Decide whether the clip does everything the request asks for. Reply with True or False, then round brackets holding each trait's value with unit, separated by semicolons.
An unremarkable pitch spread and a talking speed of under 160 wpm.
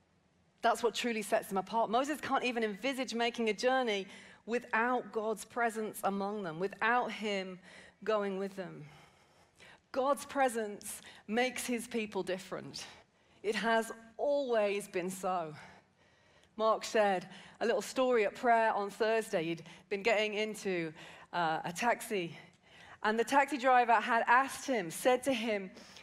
True (3.6 semitones; 140 wpm)